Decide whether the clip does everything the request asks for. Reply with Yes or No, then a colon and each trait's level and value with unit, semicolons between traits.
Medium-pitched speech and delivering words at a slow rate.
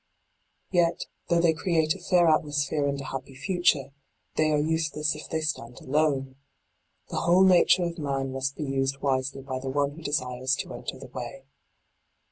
No: medium, 145 Hz; average, 175 wpm